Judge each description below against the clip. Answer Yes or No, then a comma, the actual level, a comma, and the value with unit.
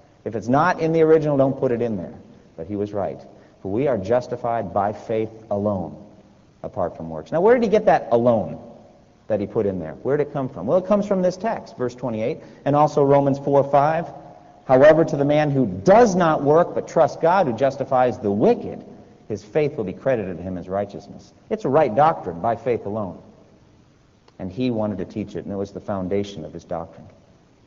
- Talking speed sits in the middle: No, fast, 215 wpm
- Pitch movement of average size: No, wide, 7.0 semitones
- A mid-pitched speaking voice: No, low, 125 Hz